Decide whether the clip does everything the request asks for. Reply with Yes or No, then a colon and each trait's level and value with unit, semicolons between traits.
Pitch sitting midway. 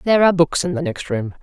Yes: medium, 165 Hz